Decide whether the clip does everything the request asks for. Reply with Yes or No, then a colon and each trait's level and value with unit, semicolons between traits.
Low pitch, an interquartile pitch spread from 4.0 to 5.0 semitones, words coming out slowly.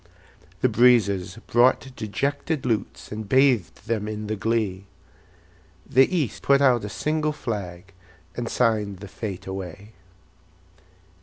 Yes: low, 110 Hz; average, 4.4 semitones; slow, 125 wpm